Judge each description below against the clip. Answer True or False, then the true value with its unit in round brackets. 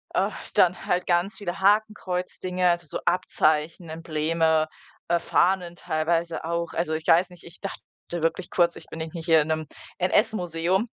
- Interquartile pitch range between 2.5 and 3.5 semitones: False (2.0 semitones)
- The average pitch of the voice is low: False (170 Hz)